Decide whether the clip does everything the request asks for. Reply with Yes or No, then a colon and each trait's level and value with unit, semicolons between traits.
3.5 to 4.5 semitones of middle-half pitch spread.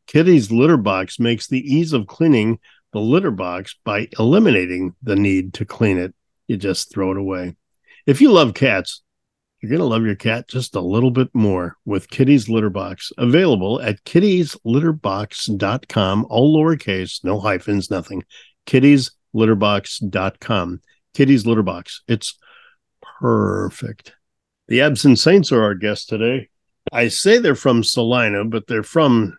No: average, 4.9 semitones